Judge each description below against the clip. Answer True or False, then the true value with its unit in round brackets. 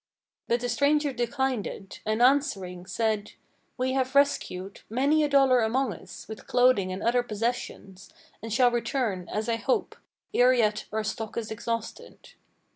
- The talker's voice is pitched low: False (235 Hz)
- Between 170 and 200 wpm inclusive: False (155 wpm)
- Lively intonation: False (3.4 semitones)